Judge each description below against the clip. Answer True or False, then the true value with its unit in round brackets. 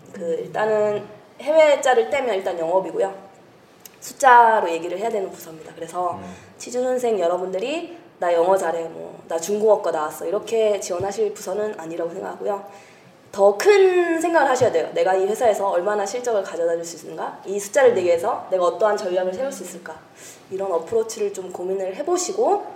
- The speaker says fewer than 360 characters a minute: False (385 characters per minute)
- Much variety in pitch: False (5.0 semitones)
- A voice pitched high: True (200 Hz)